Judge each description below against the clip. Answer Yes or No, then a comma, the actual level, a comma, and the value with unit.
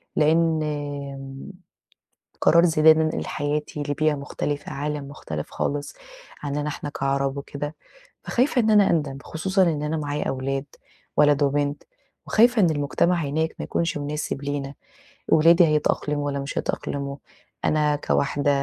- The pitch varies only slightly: Yes, narrow, 1.9 semitones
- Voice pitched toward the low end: No, medium, 145 Hz